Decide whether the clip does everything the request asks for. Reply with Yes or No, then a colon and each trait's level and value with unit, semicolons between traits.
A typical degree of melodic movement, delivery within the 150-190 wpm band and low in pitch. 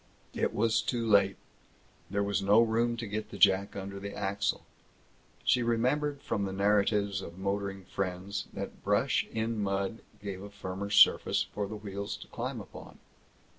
No: narrow, 2.0 semitones; average, 165 wpm; low, 100 Hz